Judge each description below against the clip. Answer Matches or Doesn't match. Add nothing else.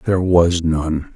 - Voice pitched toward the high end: Doesn't match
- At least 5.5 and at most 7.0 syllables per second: Doesn't match